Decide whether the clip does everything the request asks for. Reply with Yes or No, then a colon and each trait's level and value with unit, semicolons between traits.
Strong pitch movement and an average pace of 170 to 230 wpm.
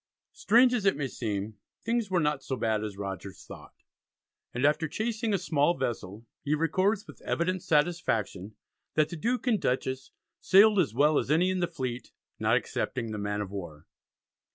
Yes: wide, 9.0 semitones; average, 175 wpm